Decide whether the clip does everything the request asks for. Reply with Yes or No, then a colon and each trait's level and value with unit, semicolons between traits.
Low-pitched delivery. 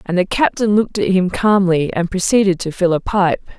No: high, 190 Hz